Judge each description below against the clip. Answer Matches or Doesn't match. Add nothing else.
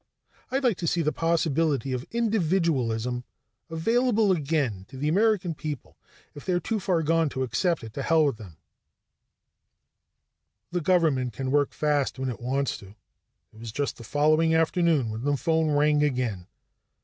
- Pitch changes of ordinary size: Matches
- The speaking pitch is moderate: Matches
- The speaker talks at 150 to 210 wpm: Matches